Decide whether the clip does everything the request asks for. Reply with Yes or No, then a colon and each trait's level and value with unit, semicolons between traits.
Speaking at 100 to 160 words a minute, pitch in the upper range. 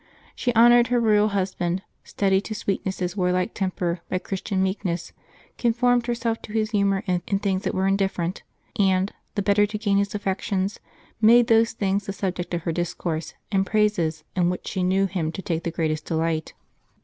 No: average, 185 wpm; high, 195 Hz